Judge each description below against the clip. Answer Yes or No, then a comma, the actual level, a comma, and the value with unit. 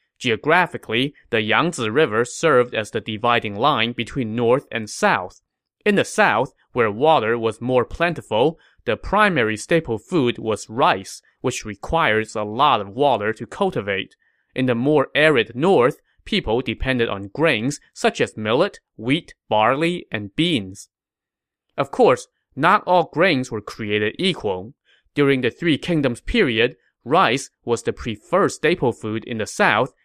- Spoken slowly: No, average, 145 wpm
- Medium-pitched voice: No, low, 120 Hz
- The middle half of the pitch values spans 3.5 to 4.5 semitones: No, wide, 5.4 semitones